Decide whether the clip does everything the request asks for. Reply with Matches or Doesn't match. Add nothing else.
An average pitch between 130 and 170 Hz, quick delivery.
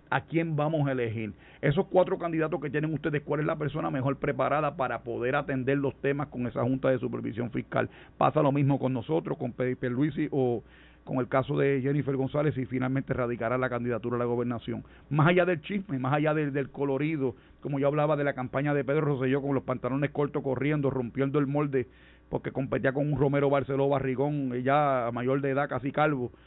Matches